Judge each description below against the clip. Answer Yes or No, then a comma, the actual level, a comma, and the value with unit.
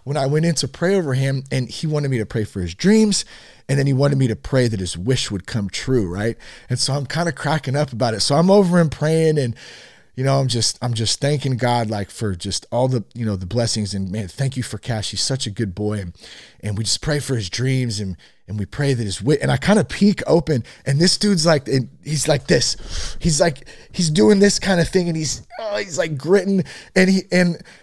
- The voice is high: No, low, 135 Hz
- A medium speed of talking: No, fast, 260 wpm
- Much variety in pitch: Yes, wide, 6.1 semitones